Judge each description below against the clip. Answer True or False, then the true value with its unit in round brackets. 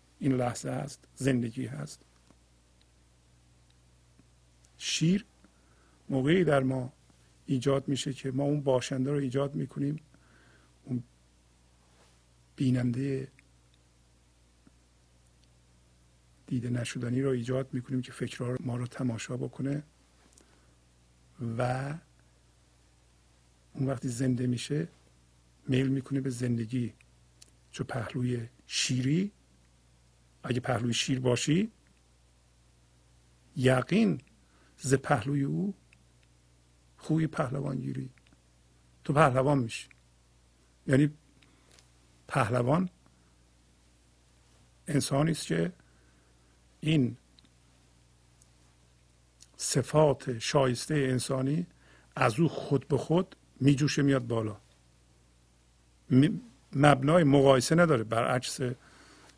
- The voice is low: True (105 Hz)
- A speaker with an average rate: False (80 wpm)